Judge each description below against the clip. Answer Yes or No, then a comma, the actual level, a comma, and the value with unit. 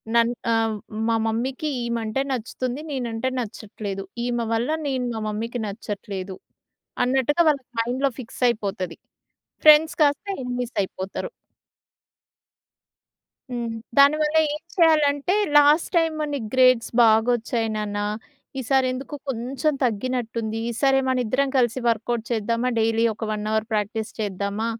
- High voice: Yes, high, 240 Hz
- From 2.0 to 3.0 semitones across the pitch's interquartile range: No, average, 3.4 semitones